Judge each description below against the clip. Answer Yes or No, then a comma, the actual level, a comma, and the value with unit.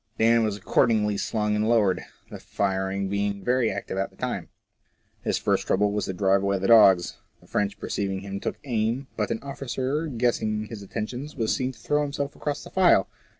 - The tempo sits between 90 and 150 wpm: No, average, 195 wpm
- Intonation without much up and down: No, average, 3.8 semitones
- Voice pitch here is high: No, low, 105 Hz